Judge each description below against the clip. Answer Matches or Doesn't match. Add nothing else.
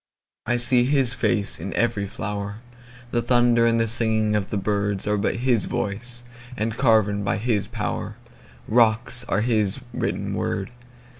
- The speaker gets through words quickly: Doesn't match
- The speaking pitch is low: Matches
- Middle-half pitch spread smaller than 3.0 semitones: Matches